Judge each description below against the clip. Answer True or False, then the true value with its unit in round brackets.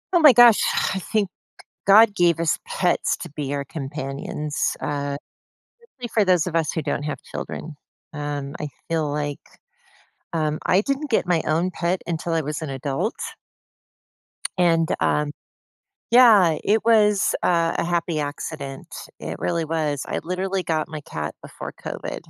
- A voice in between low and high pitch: True (165 Hz)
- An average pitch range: True (3.9 semitones)